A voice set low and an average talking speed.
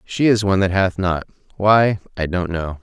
No: very low, 95 Hz; fast, 210 wpm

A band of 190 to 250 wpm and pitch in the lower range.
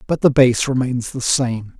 Yes: average, 200 wpm; low, 125 Hz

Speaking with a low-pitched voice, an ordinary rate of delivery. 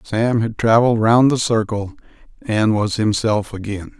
Yes: low, 110 Hz; average, 150 wpm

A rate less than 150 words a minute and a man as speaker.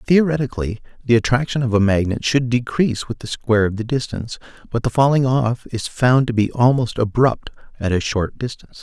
No: average, 190 wpm; male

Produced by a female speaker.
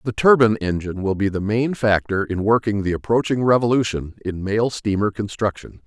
No: male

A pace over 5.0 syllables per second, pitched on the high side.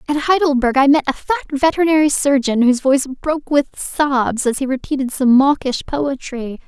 Yes: 5.5 syllables/s; very high, 275 Hz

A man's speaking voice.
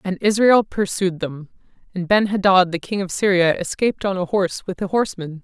No: female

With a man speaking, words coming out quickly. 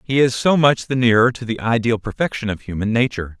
Yes: male; fast, 230 wpm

